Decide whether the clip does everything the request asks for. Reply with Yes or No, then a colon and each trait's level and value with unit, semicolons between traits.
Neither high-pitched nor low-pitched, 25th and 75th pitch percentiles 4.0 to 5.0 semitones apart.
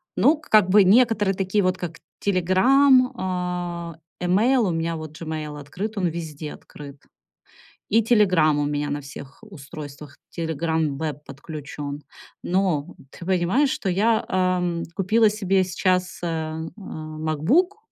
Yes: medium, 180 Hz; average, 4.4 semitones